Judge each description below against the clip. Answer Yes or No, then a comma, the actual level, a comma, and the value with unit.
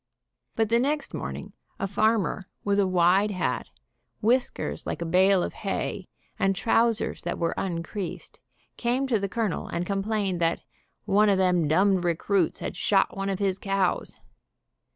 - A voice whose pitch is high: Yes, high, 195 Hz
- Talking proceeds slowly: No, average, 155 wpm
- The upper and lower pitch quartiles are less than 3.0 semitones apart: Yes, narrow, 2.6 semitones